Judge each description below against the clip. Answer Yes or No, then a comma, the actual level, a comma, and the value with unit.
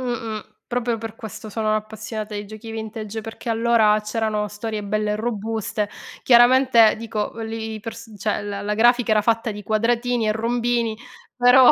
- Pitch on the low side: No, high, 220 Hz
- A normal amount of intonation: No, narrow, 1.6 semitones